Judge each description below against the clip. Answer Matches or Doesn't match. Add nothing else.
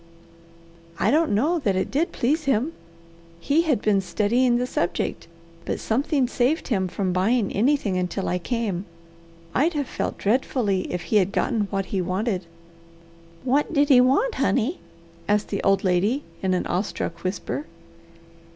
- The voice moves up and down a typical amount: Doesn't match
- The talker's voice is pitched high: Matches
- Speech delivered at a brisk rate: Doesn't match